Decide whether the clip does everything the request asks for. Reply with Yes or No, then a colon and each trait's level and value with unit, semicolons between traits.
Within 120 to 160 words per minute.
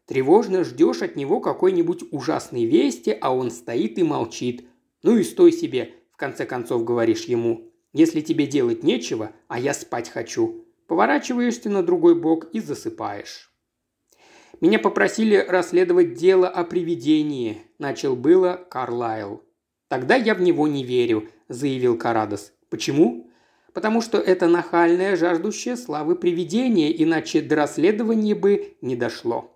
Yes: average, 135 wpm